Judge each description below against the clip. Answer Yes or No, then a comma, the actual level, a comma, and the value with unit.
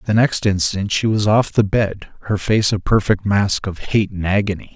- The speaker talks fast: Yes, fast, 215 wpm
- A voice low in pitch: Yes, low, 100 Hz